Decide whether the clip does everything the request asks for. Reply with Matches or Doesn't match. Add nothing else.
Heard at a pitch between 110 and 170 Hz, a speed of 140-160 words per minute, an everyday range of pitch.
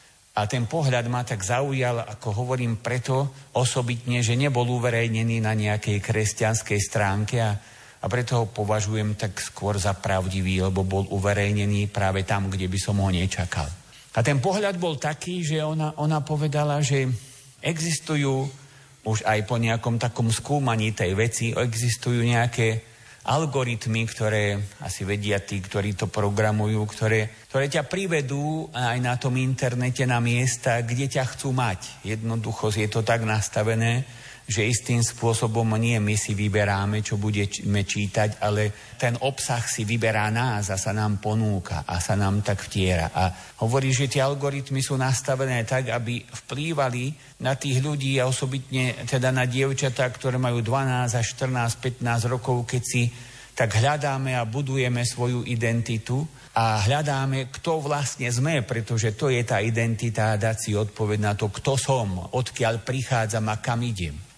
Matches